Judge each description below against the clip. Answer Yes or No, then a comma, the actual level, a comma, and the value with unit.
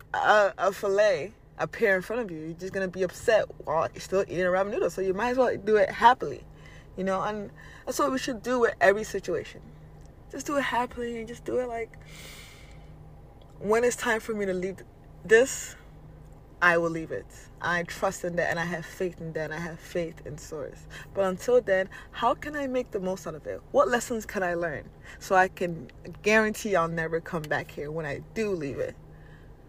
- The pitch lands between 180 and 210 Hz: Yes, high, 190 Hz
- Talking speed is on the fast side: Yes, fast, 215 wpm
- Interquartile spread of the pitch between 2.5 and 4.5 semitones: No, average, 5.0 semitones